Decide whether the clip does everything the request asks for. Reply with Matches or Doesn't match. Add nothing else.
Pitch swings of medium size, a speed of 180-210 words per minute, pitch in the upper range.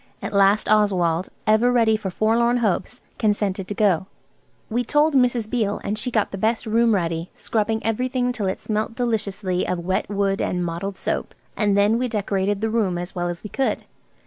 Matches